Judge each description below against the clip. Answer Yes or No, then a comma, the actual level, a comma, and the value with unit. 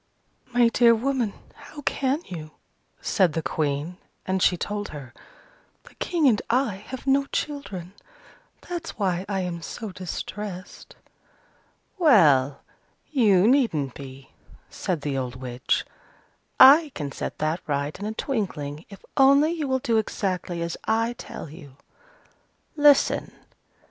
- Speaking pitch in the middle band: No, high, 195 Hz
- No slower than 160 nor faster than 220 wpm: No, slow, 135 wpm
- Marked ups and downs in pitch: Yes, wide, 9.0 semitones